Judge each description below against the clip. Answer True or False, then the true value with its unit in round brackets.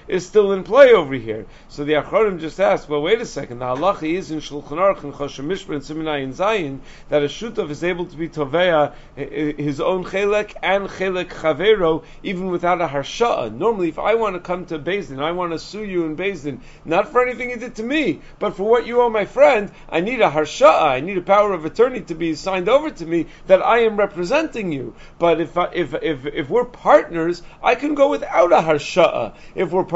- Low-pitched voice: False (175 Hz)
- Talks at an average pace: False (215 wpm)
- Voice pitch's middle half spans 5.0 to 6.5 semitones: True (5.3 semitones)